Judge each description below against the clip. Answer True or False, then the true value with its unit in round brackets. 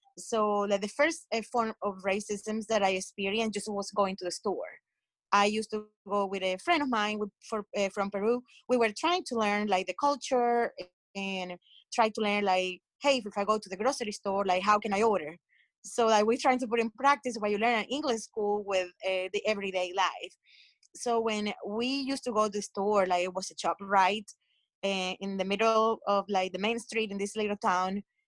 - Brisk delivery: True (220 wpm)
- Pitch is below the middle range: False (210 Hz)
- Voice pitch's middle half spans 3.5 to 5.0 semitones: False (2.6 semitones)